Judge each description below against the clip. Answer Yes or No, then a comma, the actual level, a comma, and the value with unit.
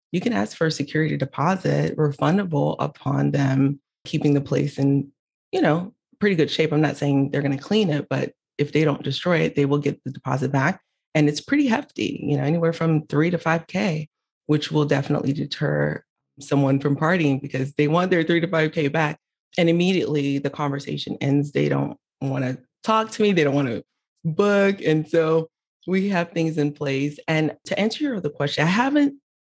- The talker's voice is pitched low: No, medium, 150 Hz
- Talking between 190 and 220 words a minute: Yes, average, 200 wpm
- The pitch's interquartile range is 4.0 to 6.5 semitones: No, average, 3.3 semitones